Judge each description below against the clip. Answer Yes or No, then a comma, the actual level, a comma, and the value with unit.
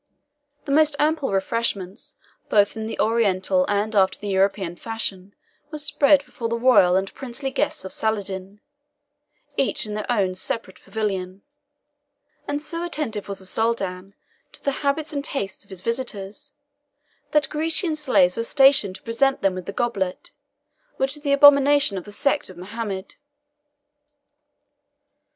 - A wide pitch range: Yes, wide, 6.3 semitones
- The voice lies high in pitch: Yes, high, 225 Hz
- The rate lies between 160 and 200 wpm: No, average, 150 wpm